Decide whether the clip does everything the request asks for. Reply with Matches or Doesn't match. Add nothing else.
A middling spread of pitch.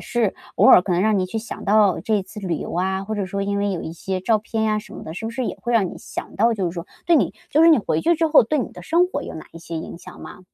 Matches